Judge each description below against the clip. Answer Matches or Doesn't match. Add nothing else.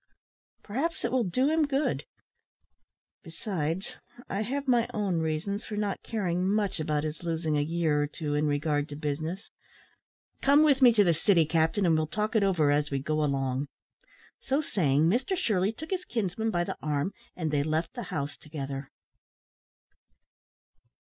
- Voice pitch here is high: Doesn't match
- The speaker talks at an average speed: Matches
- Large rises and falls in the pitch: Matches